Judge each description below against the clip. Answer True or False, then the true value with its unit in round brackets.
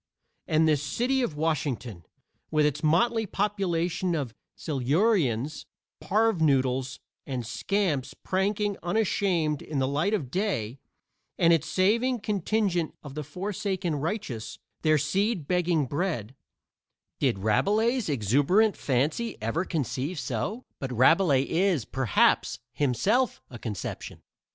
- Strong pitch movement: True (6.7 semitones)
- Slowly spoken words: True (115 wpm)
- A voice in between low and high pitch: True (160 Hz)